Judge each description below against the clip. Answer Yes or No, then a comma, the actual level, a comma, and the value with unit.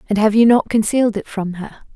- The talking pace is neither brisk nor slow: No, fast, 245 wpm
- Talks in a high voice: Yes, high, 215 Hz